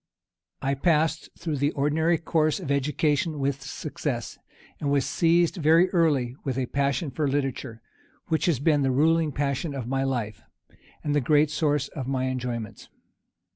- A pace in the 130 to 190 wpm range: Yes, average, 160 wpm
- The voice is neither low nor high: Yes, medium, 145 Hz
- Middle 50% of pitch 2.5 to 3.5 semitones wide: Yes, average, 2.8 semitones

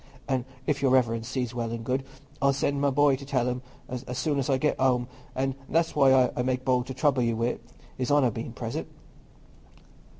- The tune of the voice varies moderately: No, narrow, 2.0 semitones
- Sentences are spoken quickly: Yes, fast, 210 wpm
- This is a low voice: Yes, low, 130 Hz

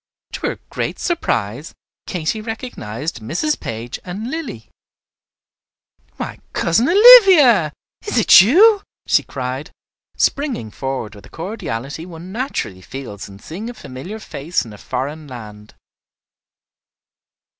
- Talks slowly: Yes, slow, 120 wpm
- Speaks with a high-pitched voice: No, medium, 160 Hz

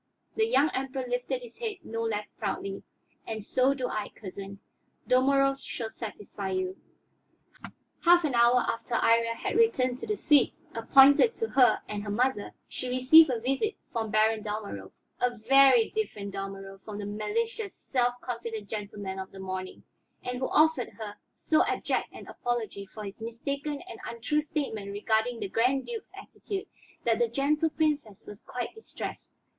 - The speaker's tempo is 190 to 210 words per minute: No, average, 160 wpm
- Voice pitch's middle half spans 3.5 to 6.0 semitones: Yes, average, 4.7 semitones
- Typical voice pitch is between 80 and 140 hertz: No, high, 240 Hz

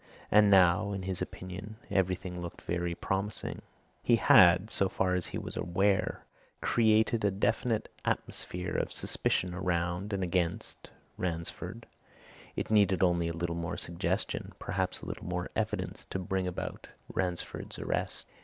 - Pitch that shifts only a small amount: Yes, narrow, 2.3 semitones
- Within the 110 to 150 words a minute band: Yes, average, 145 wpm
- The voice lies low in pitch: Yes, very low, 90 Hz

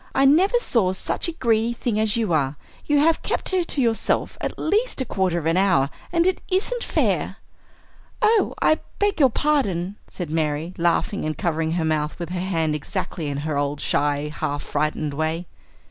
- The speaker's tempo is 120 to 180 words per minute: No, average, 190 wpm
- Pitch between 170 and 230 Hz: Yes, medium, 185 Hz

